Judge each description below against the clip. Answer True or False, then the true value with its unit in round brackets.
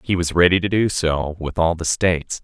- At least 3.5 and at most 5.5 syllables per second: True (5.2 syllables/s)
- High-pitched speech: False (85 Hz)